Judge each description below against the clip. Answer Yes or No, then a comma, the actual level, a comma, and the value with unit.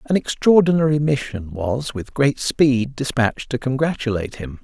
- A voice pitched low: Yes, low, 130 Hz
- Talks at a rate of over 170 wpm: No, average, 140 wpm